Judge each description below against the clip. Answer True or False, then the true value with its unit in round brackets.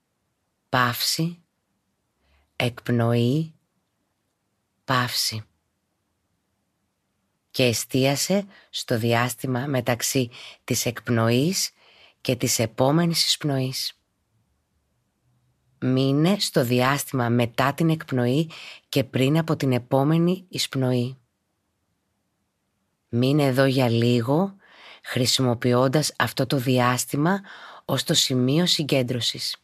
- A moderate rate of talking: False (75 wpm)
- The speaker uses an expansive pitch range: False (3.9 semitones)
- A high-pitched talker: False (125 Hz)